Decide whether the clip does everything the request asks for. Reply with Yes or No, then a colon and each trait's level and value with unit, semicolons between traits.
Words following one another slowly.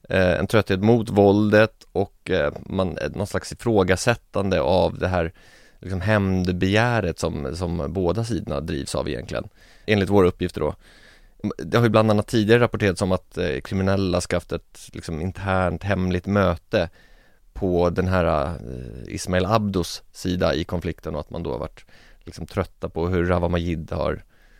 No: average, 150 wpm